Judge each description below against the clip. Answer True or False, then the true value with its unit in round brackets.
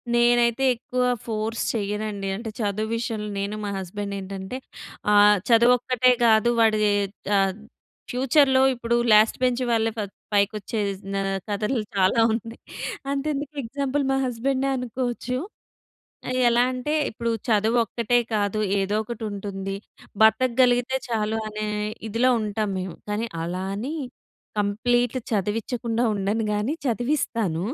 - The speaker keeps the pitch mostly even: False (3.0 semitones)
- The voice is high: True (225 Hz)